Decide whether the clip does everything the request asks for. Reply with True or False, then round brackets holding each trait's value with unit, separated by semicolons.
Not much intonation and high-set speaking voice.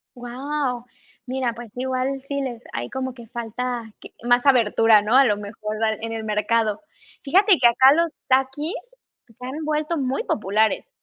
False (3.2 semitones; 250 Hz)